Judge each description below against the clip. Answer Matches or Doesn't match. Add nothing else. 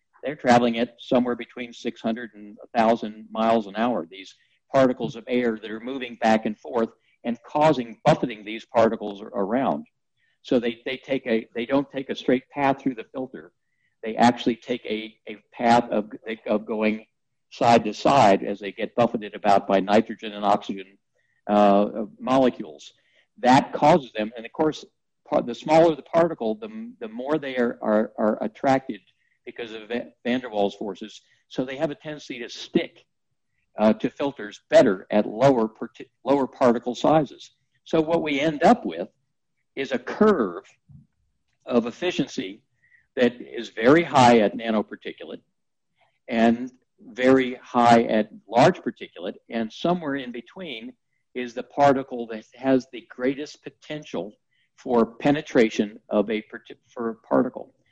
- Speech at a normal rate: Matches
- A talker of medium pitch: Doesn't match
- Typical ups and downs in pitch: Matches